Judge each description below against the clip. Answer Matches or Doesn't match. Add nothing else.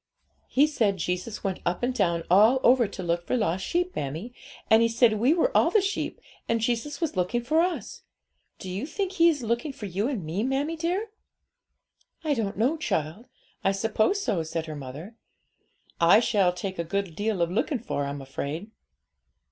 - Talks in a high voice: Matches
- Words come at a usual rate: Matches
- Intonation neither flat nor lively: Doesn't match